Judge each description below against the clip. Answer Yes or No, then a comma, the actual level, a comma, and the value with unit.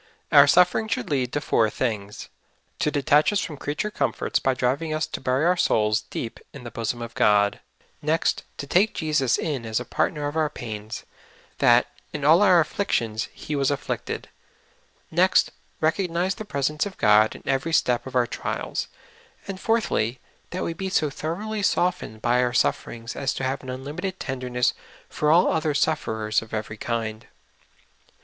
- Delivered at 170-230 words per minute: Yes, average, 185 wpm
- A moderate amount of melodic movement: No, wide, 5.7 semitones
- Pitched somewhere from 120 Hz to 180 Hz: Yes, medium, 140 Hz